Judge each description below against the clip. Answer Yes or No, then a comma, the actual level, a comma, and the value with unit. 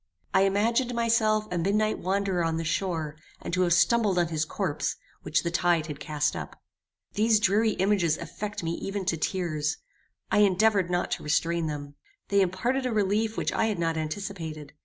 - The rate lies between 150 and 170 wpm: No, average, 180 wpm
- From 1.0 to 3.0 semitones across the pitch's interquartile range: No, average, 4.3 semitones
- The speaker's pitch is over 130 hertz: Yes, medium, 185 Hz